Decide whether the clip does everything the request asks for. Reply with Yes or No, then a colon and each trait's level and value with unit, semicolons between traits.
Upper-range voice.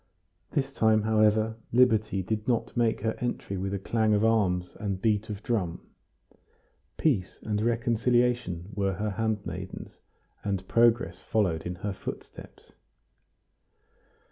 No: low, 110 Hz